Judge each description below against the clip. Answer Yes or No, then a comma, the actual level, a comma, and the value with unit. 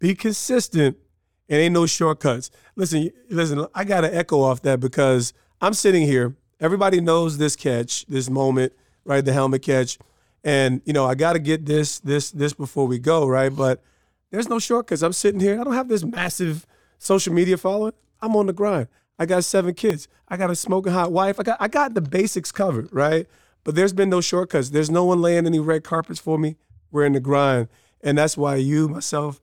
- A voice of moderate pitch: Yes, medium, 160 Hz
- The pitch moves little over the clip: No, average, 5.1 semitones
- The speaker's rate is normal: No, fast, 210 wpm